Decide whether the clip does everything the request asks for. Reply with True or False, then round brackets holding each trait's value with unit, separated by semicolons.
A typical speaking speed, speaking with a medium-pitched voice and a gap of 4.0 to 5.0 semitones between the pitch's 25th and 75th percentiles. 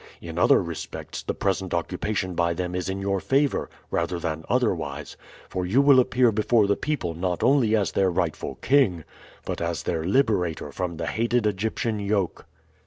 False (175 wpm; 95 Hz; 4.6 semitones)